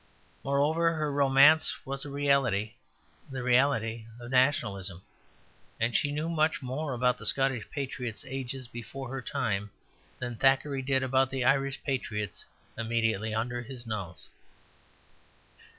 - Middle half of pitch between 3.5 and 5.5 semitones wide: No, average, 3.1 semitones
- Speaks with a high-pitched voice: No, low, 130 Hz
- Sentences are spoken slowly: Yes, slow, 130 wpm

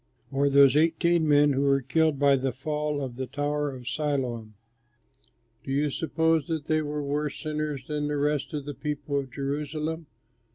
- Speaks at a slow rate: No, average, 175 wpm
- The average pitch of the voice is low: No, medium, 145 Hz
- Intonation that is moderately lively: No, narrow, 1.7 semitones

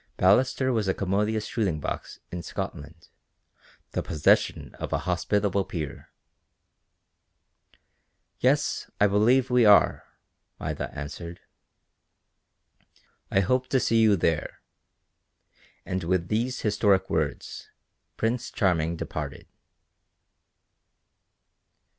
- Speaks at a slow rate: Yes, slow, 95 wpm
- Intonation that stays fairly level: No, average, 4.7 semitones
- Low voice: Yes, low, 100 Hz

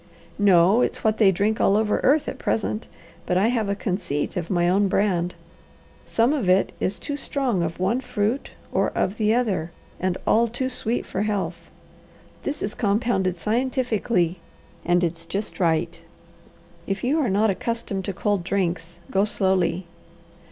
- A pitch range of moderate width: Yes, average, 4.0 semitones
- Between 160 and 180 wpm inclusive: Yes, average, 165 wpm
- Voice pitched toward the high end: Yes, high, 200 Hz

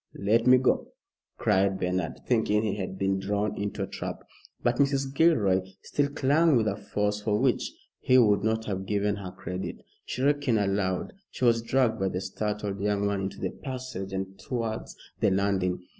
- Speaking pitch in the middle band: No, low, 105 Hz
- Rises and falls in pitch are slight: No, average, 4.0 semitones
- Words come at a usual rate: Yes, average, 175 wpm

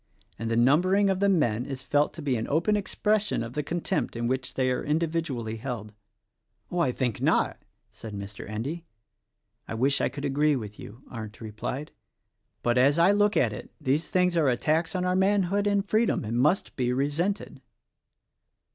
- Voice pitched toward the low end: No, medium, 145 Hz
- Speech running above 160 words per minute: Yes, average, 180 wpm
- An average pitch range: No, wide, 6.9 semitones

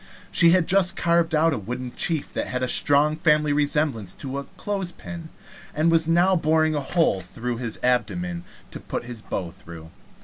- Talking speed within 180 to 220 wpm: Yes, average, 190 wpm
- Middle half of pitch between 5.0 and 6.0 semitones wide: Yes, wide, 5.5 semitones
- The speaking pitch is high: No, medium, 150 Hz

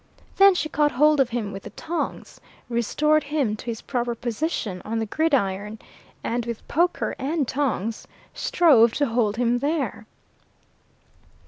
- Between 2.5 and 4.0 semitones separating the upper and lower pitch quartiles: No, average, 5.2 semitones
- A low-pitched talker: No, high, 245 Hz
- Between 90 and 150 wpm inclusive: Yes, average, 145 wpm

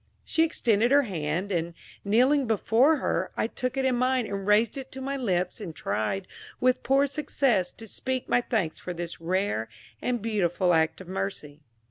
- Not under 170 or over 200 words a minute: Yes, average, 180 wpm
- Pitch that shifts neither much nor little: No, wide, 6.2 semitones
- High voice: Yes, high, 210 Hz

